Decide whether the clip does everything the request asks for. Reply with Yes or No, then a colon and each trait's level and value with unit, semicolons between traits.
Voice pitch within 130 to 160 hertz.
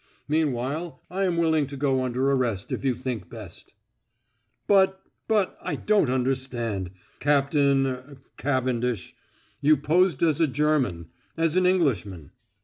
Yes: medium, 140 Hz